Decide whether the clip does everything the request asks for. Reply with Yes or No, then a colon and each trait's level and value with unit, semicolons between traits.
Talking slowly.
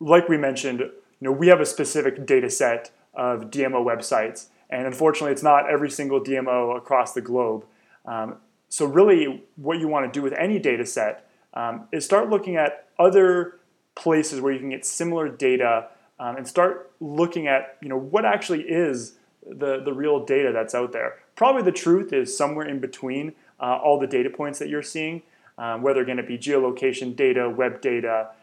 No: average, 195 wpm